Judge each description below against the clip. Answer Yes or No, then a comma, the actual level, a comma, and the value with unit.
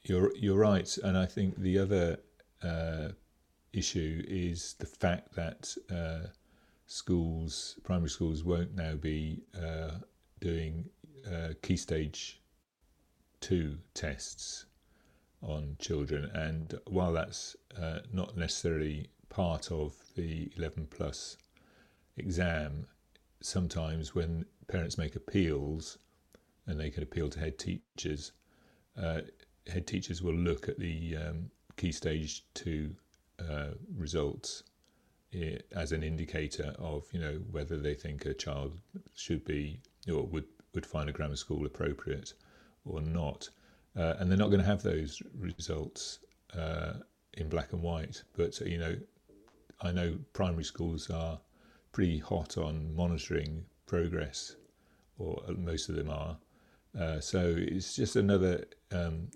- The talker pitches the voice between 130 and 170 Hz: No, very low, 80 Hz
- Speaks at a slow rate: Yes, slow, 130 wpm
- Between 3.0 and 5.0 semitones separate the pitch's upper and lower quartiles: No, narrow, 2.5 semitones